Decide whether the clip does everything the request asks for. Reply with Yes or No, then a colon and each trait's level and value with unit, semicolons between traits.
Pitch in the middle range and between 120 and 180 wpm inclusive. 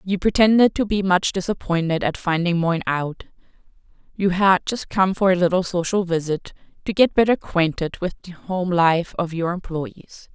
Yes: medium, 180 Hz; average, 170 wpm